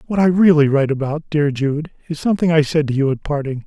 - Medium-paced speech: No, fast, 245 wpm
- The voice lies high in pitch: No, medium, 150 Hz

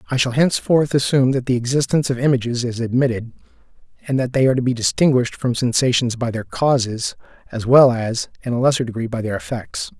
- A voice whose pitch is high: No, low, 125 Hz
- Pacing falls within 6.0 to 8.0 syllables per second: Yes, 6.4 syllables/s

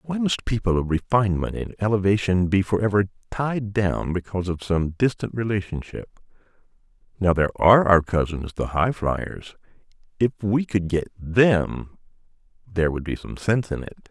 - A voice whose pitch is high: No, low, 100 Hz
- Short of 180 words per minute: Yes, average, 150 wpm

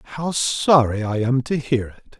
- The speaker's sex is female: No, male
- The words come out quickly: No, average, 190 wpm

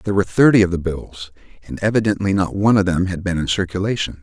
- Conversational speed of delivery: No, fast, 225 wpm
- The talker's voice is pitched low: Yes, very low, 95 Hz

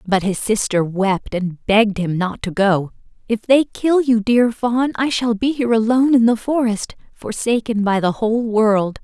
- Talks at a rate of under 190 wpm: No, average, 195 wpm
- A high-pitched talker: Yes, high, 220 Hz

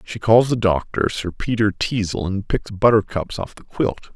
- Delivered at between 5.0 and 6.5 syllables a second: No, 4.6 syllables/s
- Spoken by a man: Yes, male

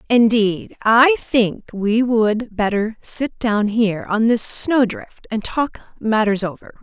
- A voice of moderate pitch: No, high, 225 Hz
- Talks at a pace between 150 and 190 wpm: No, average, 140 wpm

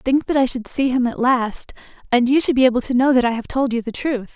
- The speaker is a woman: Yes, female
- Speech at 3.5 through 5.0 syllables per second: No, 6.1 syllables/s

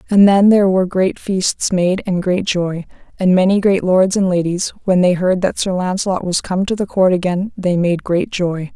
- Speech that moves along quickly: Yes, fast, 220 wpm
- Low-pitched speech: No, medium, 185 Hz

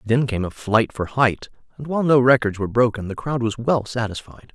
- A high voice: No, low, 120 Hz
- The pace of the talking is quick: Yes, fast, 225 wpm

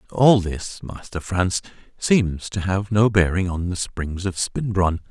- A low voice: Yes, very low, 95 Hz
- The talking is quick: No, average, 165 wpm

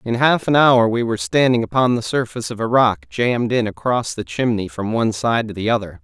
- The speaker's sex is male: Yes, male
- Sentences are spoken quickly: Yes, fast, 240 wpm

